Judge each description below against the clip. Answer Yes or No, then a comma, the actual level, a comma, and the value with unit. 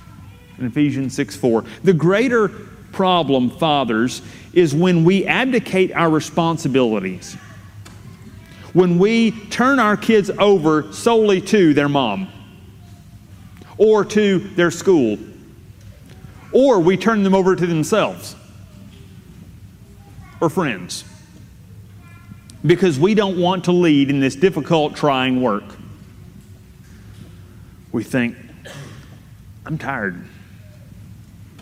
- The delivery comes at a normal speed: No, slow, 100 wpm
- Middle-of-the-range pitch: No, low, 130 Hz